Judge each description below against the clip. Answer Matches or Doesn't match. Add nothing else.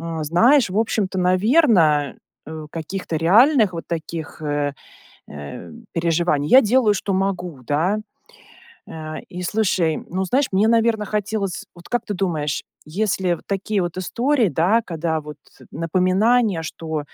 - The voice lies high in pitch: Doesn't match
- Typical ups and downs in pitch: Matches